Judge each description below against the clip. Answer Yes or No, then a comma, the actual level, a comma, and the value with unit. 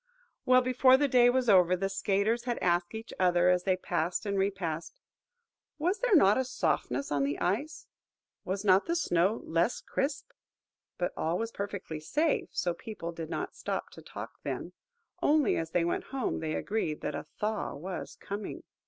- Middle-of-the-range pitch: No, high, 195 Hz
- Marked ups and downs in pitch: Yes, wide, 6.1 semitones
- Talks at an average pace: Yes, average, 175 wpm